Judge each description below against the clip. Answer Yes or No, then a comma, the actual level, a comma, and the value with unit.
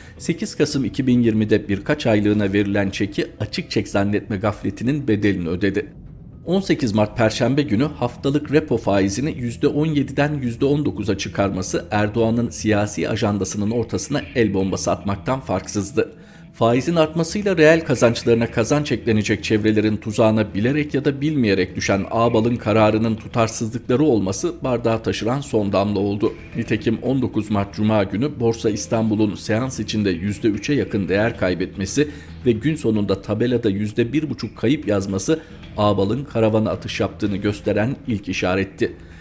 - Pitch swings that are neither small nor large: Yes, average, 4.0 semitones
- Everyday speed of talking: Yes, average, 120 wpm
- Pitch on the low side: Yes, low, 110 Hz